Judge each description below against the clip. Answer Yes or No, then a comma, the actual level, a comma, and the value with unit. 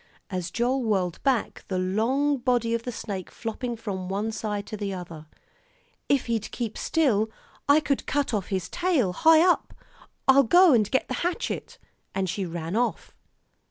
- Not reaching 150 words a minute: No, average, 175 wpm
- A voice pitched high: Yes, high, 225 Hz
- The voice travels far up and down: Yes, wide, 5.7 semitones